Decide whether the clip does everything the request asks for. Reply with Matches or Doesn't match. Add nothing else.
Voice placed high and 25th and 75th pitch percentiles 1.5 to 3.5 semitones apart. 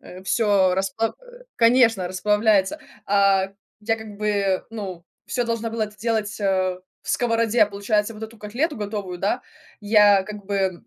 Matches